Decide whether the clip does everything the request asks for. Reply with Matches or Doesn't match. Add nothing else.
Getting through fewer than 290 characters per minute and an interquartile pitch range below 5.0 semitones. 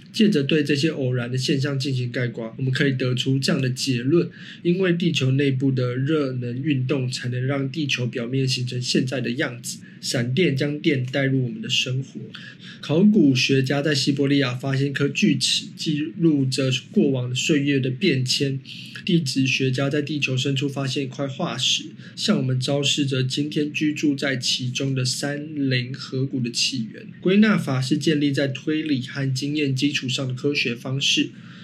Matches